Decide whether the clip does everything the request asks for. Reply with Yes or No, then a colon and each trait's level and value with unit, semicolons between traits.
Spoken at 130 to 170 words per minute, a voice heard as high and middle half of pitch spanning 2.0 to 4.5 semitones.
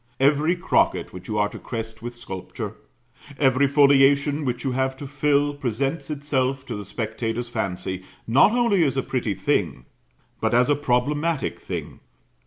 No: average, 160 wpm; low, 135 Hz; average, 4.0 semitones